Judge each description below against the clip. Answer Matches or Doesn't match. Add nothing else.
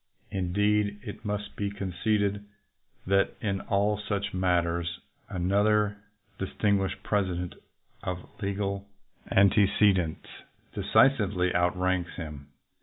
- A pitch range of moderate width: Doesn't match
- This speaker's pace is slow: Matches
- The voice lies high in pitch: Doesn't match